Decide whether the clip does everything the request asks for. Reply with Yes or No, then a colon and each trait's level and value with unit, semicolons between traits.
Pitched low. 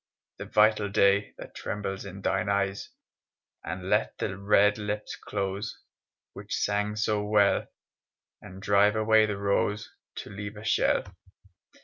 Yes: low, 105 Hz